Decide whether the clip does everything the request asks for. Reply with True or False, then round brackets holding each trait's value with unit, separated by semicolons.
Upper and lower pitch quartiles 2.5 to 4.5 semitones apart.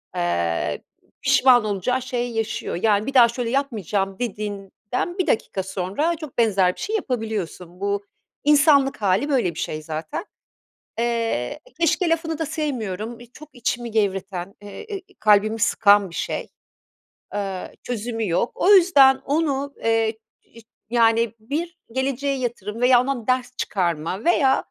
False (5.3 semitones)